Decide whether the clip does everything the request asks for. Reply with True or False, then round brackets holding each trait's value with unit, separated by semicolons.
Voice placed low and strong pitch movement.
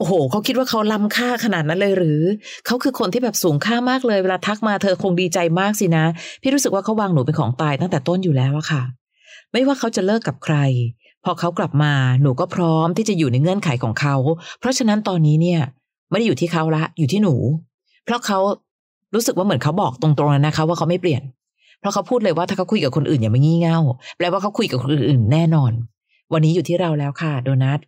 False (170 Hz; 5.7 semitones)